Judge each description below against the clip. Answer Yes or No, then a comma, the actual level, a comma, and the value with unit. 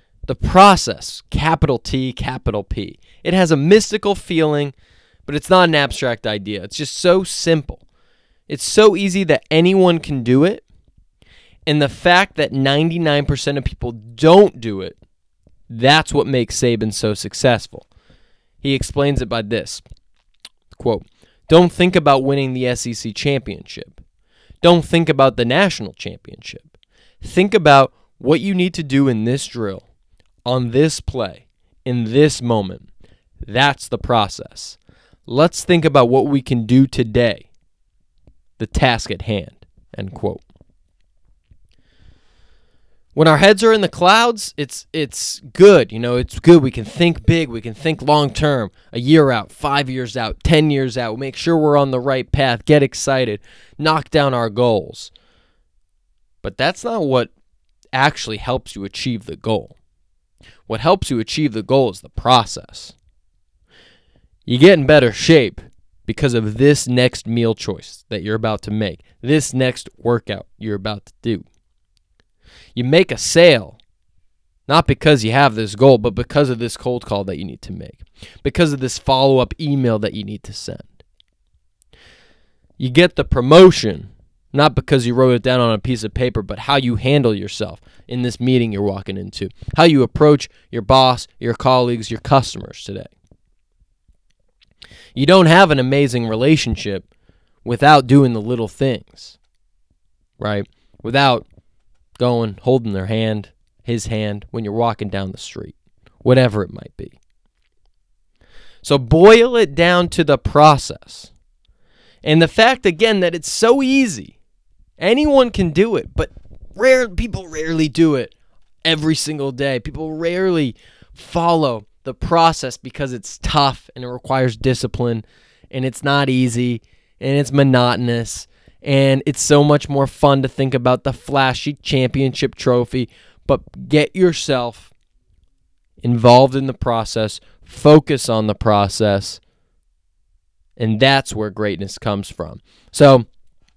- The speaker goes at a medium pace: Yes, average, 150 wpm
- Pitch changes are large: Yes, wide, 5.7 semitones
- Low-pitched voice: Yes, low, 125 Hz